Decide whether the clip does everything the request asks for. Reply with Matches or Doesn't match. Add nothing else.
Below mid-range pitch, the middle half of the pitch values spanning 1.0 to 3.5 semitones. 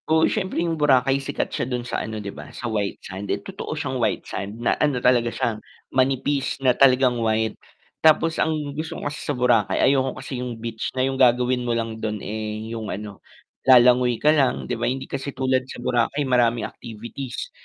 Matches